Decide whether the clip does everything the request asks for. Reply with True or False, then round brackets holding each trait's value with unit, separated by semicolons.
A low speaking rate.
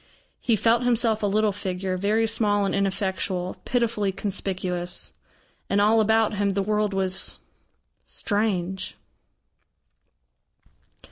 True (110 wpm)